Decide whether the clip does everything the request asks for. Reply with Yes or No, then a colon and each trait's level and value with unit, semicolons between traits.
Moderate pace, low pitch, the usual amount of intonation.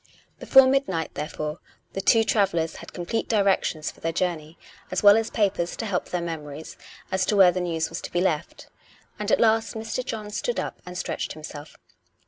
No: average, 195 wpm; medium, 185 Hz; average, 4.9 semitones